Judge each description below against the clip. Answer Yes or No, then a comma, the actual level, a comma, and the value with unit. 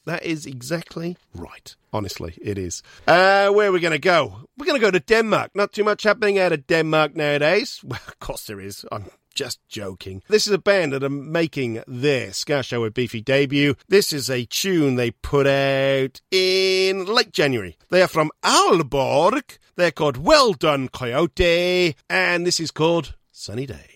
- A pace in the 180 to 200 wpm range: Yes, average, 185 wpm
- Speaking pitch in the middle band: Yes, medium, 155 Hz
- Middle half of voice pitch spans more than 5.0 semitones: Yes, wide, 5.6 semitones